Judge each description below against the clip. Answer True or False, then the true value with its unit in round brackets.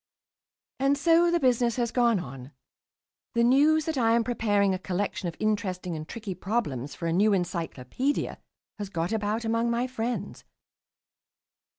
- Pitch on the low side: False (220 Hz)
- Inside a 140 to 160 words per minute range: True (155 wpm)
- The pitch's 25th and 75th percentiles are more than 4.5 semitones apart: True (5.2 semitones)